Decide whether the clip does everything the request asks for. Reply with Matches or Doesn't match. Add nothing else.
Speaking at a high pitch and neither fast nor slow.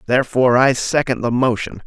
Doesn't match